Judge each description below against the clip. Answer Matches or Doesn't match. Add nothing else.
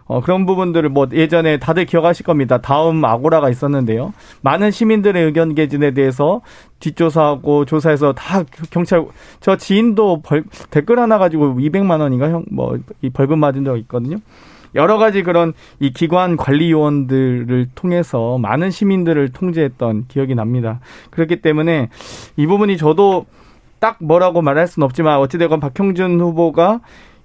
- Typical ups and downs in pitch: Matches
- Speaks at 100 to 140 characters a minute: Doesn't match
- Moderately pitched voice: Matches